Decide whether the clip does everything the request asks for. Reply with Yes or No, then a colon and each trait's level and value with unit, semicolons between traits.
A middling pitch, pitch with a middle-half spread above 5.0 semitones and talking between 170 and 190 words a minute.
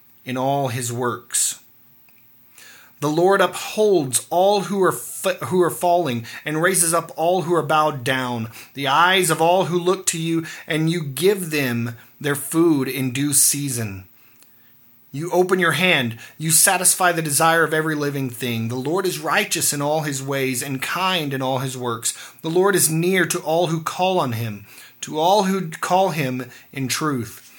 Yes: medium, 155 Hz; wide, 5.4 semitones; average, 180 wpm